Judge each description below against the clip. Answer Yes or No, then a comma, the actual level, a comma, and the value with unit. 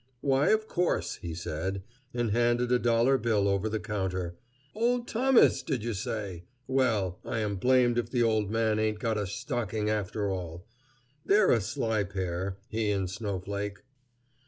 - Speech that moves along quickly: No, average, 160 wpm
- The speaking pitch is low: Yes, low, 110 Hz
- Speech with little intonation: No, average, 3.6 semitones